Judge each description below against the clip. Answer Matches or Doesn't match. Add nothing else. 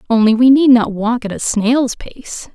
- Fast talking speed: Matches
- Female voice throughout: Matches